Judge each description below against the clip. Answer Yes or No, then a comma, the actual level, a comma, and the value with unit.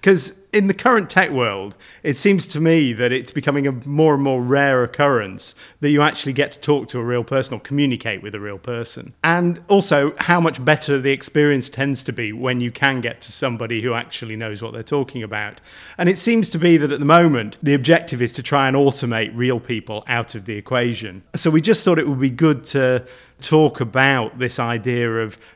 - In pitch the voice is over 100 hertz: Yes, low, 135 Hz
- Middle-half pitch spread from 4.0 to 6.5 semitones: Yes, average, 4.4 semitones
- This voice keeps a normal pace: No, fast, 220 wpm